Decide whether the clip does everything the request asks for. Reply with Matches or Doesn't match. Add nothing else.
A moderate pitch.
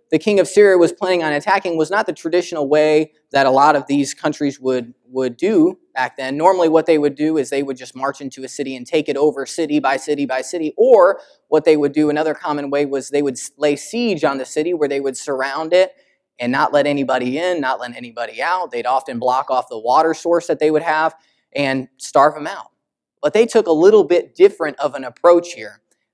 Matches